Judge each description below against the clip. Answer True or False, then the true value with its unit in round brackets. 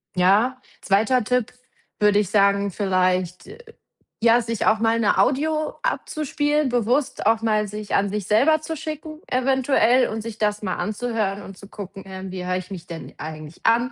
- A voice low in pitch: False (215 Hz)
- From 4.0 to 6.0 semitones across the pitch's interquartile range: True (4.4 semitones)